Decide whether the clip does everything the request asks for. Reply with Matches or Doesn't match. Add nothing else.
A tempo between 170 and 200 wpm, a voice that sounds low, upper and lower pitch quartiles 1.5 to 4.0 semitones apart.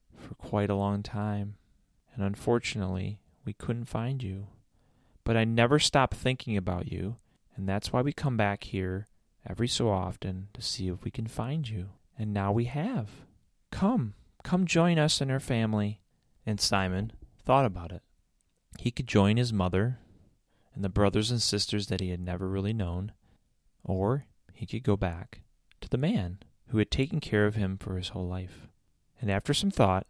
Matches